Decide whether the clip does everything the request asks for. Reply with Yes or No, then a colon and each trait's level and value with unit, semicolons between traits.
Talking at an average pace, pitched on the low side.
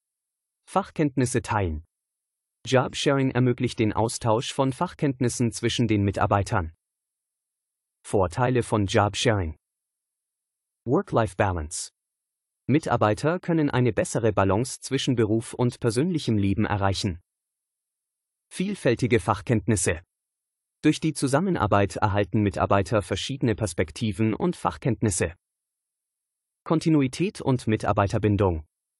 No: slow, 85 wpm; low, 115 Hz